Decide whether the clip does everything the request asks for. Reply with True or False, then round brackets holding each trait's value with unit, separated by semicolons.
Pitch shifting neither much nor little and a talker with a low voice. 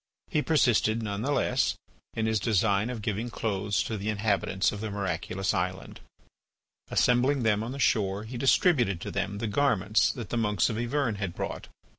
True (3.0 semitones; 110 Hz)